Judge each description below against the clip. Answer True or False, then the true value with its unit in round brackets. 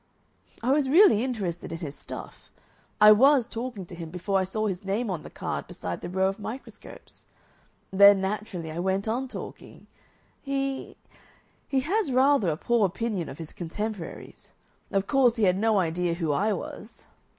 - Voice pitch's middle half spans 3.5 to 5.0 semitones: False (5.6 semitones)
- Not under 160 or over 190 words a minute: True (175 wpm)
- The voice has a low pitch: False (205 Hz)